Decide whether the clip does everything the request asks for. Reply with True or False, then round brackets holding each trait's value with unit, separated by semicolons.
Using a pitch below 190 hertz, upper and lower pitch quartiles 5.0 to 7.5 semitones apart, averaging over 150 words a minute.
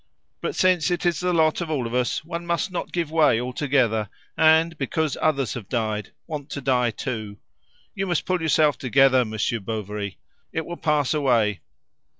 True (140 Hz; 5.6 semitones; 175 wpm)